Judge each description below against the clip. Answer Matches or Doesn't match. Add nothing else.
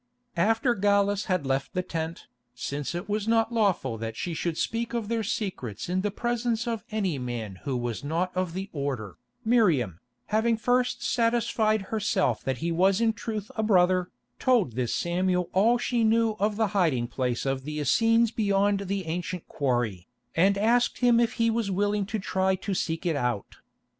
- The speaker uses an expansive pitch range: Matches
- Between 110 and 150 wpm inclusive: Doesn't match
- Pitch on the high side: Matches